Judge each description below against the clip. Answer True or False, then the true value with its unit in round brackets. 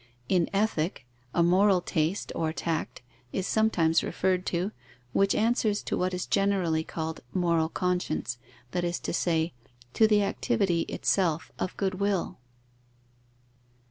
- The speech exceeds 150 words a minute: False (135 wpm)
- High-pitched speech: False (180 Hz)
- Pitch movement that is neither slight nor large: True (3.2 semitones)